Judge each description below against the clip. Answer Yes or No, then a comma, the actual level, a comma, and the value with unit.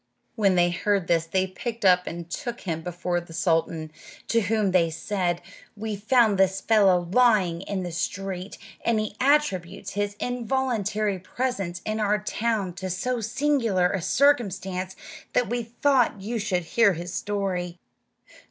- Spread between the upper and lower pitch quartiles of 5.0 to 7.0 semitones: No, average, 4.0 semitones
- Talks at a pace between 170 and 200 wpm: No, average, 155 wpm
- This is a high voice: Yes, high, 195 Hz